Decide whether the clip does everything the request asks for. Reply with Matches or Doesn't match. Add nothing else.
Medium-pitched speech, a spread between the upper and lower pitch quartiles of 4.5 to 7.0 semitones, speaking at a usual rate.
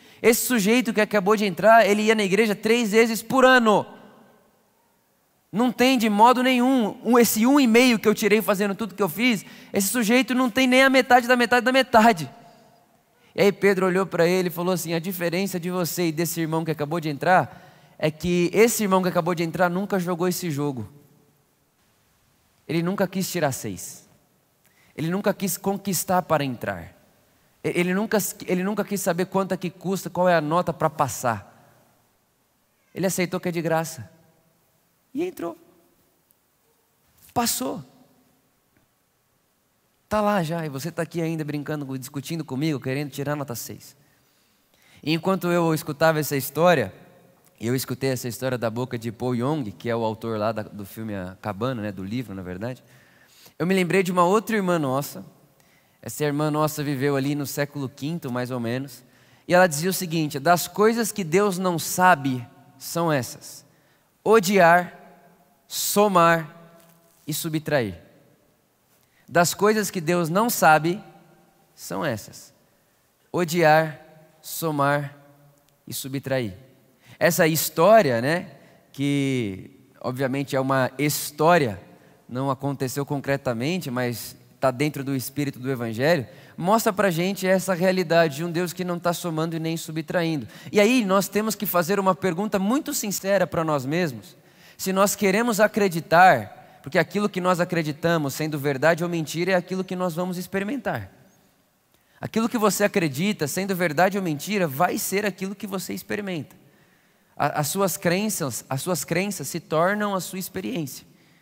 Matches